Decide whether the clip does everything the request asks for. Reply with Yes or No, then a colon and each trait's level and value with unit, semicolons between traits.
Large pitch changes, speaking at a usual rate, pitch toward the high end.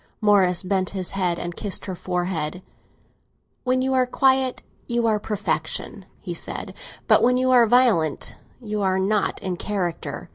No: average, 5.0 semitones; average, 155 wpm; high, 205 Hz